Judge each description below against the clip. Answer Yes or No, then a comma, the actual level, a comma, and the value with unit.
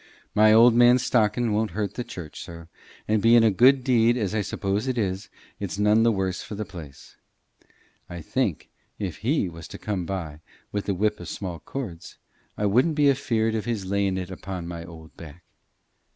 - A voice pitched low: Yes, low, 105 Hz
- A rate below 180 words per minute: No, average, 195 wpm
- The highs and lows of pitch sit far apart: No, average, 4.0 semitones